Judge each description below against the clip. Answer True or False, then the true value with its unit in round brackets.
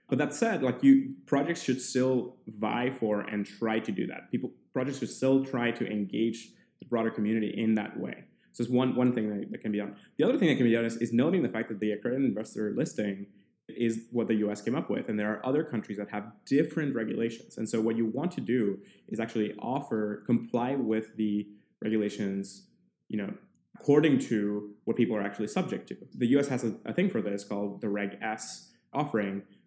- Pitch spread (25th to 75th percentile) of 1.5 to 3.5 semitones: True (3.0 semitones)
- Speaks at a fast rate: True (215 wpm)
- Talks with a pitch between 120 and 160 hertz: False (110 Hz)